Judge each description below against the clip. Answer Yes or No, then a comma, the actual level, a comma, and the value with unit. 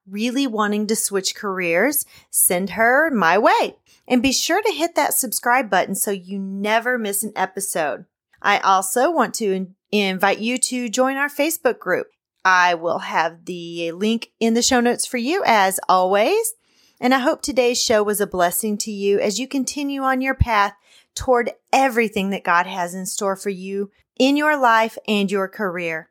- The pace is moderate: Yes, average, 180 wpm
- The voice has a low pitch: No, high, 215 Hz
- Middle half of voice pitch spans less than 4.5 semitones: No, average, 4.8 semitones